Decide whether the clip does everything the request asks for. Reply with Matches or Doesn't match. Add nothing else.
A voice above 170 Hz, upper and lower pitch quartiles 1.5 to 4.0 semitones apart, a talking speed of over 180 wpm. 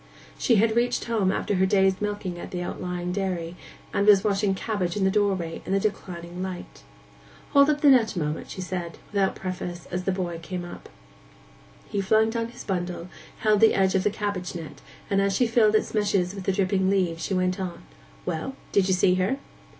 Matches